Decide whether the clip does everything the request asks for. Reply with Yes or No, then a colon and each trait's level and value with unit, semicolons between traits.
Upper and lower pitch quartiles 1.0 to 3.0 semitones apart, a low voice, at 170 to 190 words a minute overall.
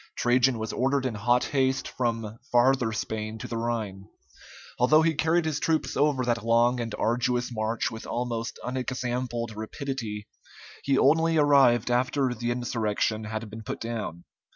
No: average, 2.7 semitones; low, 120 Hz; average, 155 wpm